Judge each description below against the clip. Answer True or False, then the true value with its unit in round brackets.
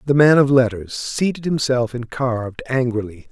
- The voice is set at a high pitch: False (125 Hz)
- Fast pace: False (165 wpm)